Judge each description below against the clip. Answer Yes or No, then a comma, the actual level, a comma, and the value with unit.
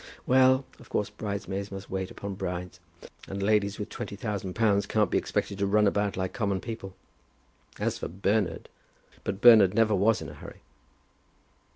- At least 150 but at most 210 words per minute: Yes, average, 170 wpm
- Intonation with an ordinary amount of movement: No, narrow, 1.9 semitones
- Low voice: Yes, low, 100 Hz